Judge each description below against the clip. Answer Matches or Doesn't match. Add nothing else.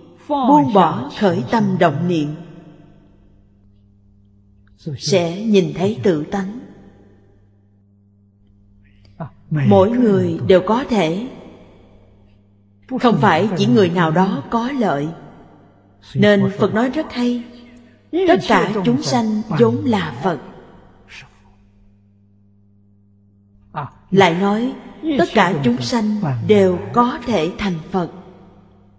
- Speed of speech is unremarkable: Doesn't match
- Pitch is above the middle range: Doesn't match